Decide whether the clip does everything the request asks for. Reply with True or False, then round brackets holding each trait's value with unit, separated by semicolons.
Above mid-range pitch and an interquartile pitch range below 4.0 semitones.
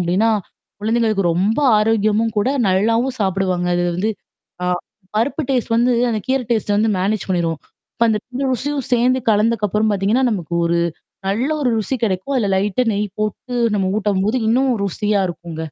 True (215 Hz; 3.3 semitones)